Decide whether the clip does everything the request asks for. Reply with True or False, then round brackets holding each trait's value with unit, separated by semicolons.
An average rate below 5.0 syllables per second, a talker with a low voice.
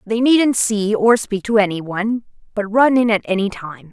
False (4.6 syllables/s; 215 Hz)